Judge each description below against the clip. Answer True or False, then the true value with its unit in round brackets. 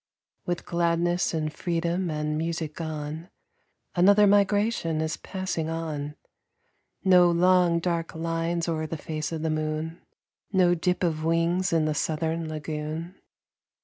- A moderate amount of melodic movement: False (2.0 semitones)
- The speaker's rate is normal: False (130 wpm)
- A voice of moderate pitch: True (165 Hz)